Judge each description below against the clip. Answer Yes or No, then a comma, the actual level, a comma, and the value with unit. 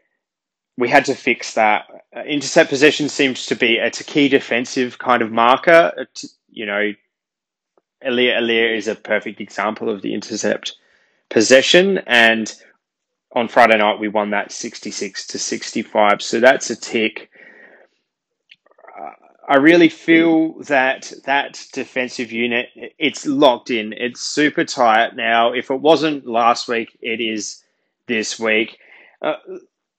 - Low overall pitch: Yes, low, 125 Hz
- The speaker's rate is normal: No, slow, 130 wpm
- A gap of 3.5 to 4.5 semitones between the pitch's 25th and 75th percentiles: Yes, average, 4.0 semitones